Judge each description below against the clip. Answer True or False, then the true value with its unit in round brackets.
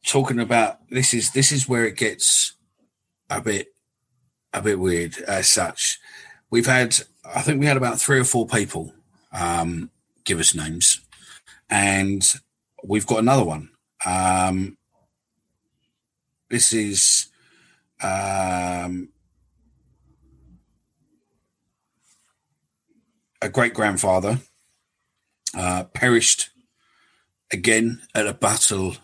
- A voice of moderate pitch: False (105 Hz)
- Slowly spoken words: True (100 wpm)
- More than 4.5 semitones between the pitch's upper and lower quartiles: True (5.4 semitones)